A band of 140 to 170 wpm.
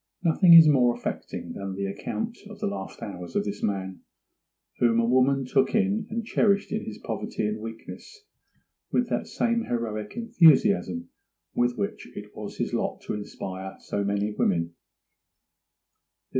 Yes: average, 155 wpm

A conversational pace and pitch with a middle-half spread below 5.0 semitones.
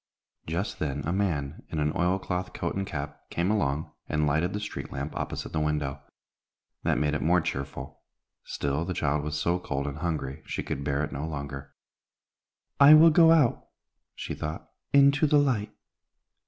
No: average, 180 wpm; average, 5.3 semitones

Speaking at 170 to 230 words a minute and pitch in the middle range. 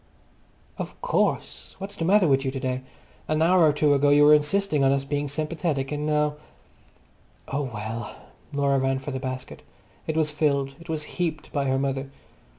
Yes: average, 185 wpm; medium, 145 Hz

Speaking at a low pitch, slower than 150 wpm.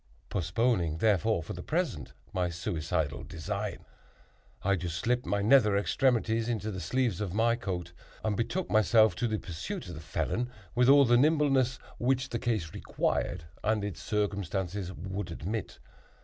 No: low, 105 Hz; average, 155 wpm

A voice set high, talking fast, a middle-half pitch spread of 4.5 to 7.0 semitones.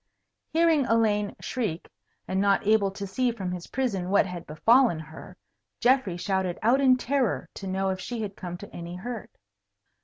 No: high, 200 Hz; average, 175 wpm; average, 4.9 semitones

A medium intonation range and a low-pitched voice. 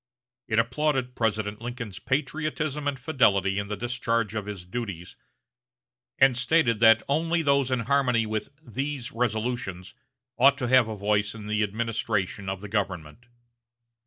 Yes: average, 4.0 semitones; low, 115 Hz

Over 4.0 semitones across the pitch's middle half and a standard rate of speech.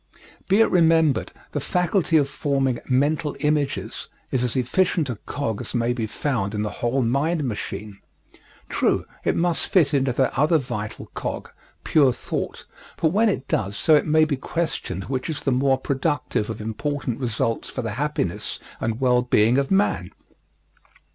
Yes: average, 4.7 semitones; average, 165 wpm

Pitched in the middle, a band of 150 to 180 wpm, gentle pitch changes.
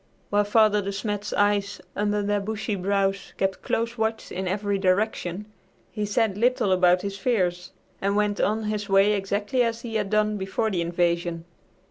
No: high, 205 Hz; average, 170 wpm; narrow, 1.7 semitones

